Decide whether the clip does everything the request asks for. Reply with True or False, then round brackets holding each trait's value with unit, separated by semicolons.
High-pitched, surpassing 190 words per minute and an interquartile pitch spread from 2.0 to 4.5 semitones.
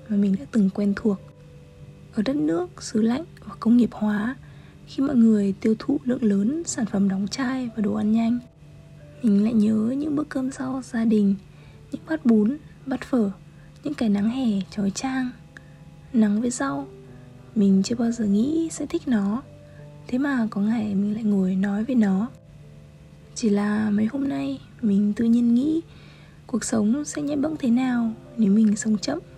False (225 Hz; 185 wpm; 4.1 semitones)